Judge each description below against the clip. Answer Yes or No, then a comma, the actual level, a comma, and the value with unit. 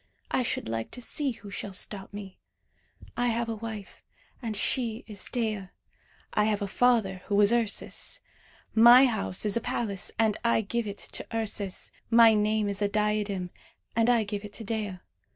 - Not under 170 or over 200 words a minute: Yes, average, 180 wpm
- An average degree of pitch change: No, narrow, 2.3 semitones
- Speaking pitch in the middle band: No, high, 215 Hz